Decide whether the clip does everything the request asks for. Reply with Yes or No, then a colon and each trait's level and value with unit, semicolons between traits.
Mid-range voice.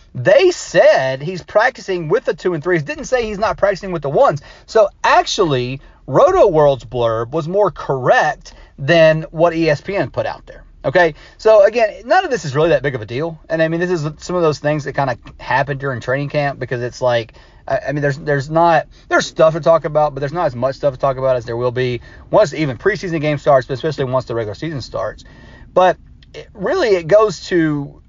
Yes: medium, 155 Hz